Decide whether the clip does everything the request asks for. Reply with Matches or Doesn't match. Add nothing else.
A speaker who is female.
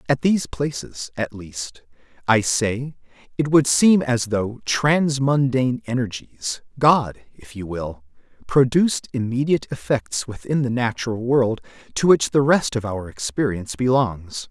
Doesn't match